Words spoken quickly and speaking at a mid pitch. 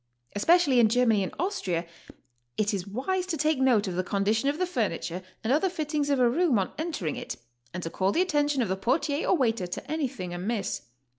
No: fast, 215 wpm; high, 245 Hz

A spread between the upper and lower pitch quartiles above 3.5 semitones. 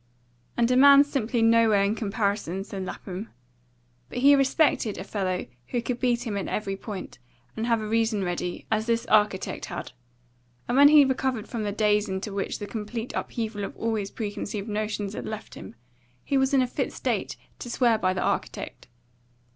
No: average, 3.1 semitones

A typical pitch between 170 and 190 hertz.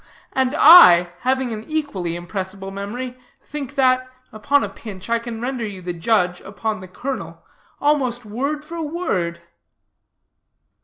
No: high, 235 Hz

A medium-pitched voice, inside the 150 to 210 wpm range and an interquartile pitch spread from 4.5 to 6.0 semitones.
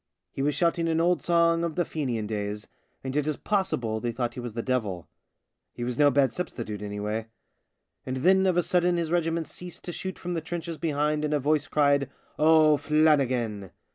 Yes: medium, 150 Hz; average, 200 wpm; wide, 5.6 semitones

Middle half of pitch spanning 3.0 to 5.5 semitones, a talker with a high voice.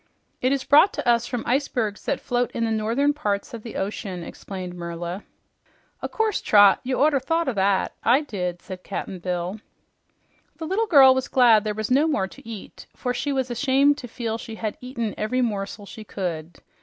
Yes: average, 4.8 semitones; high, 230 Hz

